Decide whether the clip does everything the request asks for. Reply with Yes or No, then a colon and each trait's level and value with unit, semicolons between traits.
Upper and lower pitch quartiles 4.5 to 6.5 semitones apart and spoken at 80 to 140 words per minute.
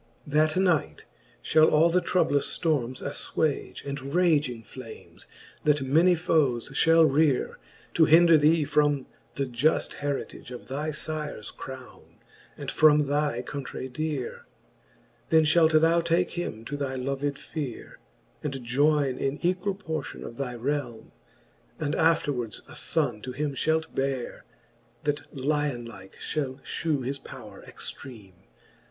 No: average, 3.2 semitones; slow, 135 wpm